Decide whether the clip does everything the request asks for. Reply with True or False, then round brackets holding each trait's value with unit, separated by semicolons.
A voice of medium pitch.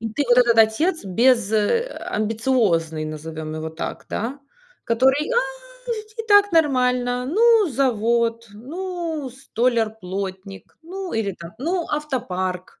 False (245 Hz)